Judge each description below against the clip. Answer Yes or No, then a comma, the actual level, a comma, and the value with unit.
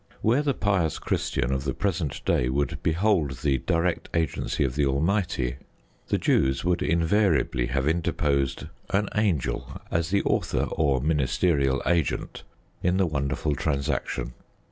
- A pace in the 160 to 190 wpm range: No, average, 140 wpm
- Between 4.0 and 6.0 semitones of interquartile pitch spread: Yes, average, 4.7 semitones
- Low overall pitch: Yes, very low, 75 Hz